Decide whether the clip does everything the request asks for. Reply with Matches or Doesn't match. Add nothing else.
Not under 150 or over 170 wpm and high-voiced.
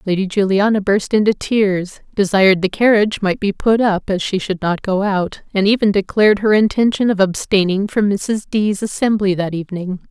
Doesn't match